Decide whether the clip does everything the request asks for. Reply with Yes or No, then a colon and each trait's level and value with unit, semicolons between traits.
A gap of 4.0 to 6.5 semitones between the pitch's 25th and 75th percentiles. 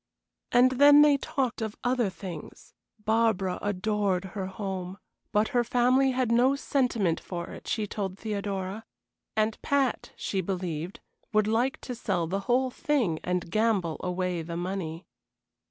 Yes: average, 4.8 semitones